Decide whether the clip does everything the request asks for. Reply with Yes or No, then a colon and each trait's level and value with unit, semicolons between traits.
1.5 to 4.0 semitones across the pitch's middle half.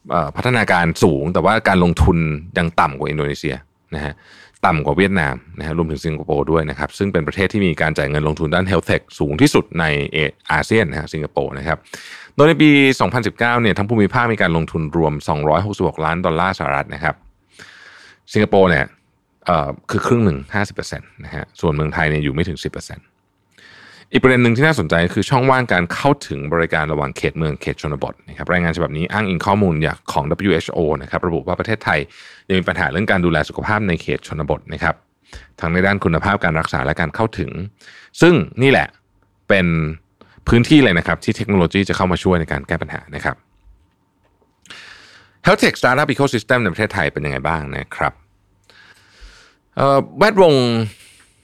No: average, 4.8 semitones